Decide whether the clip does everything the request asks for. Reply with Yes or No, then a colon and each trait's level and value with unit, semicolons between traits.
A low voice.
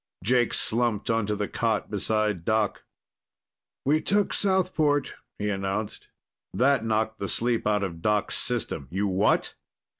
Yes: low, 110 Hz